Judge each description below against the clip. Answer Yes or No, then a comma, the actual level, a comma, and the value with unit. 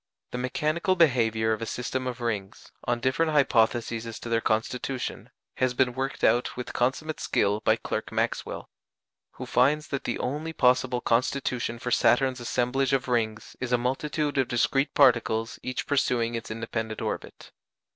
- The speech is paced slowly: No, average, 160 wpm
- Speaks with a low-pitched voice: Yes, low, 125 Hz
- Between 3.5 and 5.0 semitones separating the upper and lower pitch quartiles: No, narrow, 2.6 semitones